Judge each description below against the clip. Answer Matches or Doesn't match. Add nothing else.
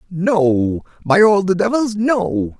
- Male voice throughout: Matches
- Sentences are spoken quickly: Doesn't match